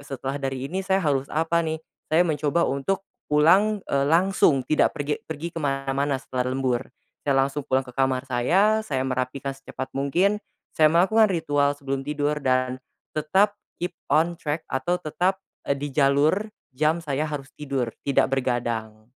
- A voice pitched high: No, medium, 145 Hz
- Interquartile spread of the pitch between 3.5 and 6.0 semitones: Yes, average, 3.9 semitones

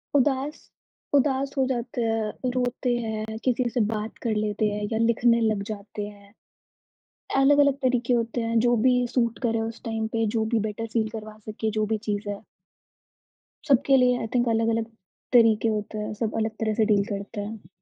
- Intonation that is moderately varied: No, narrow, 2.3 semitones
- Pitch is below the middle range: No, high, 225 Hz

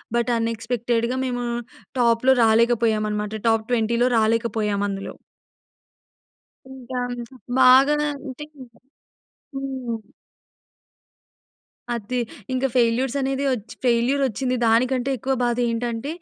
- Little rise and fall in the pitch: Yes, narrow, 2.2 semitones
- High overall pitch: Yes, high, 240 Hz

